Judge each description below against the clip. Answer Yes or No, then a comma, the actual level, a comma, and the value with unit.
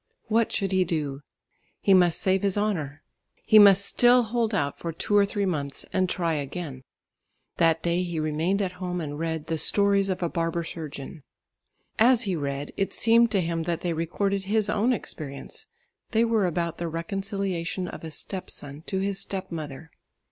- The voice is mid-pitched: Yes, medium, 180 Hz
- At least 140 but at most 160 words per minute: No, average, 185 wpm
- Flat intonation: No, average, 3.7 semitones